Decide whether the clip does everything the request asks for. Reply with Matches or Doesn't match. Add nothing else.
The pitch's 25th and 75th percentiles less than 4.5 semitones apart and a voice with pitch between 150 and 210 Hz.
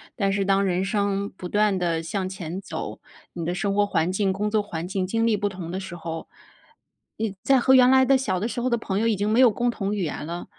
Matches